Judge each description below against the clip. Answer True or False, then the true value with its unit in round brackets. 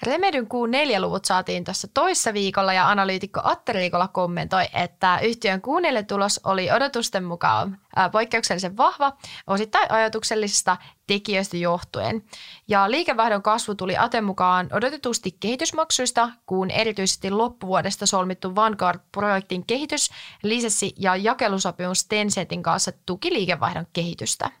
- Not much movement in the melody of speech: False (3.8 semitones)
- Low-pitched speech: False (200 Hz)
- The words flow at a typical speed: True (115 wpm)